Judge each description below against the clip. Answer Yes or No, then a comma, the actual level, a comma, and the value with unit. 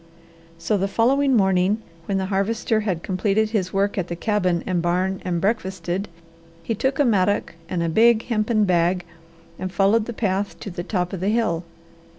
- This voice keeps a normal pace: Yes, average, 180 wpm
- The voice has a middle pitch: No, high, 195 Hz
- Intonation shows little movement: No, average, 3.1 semitones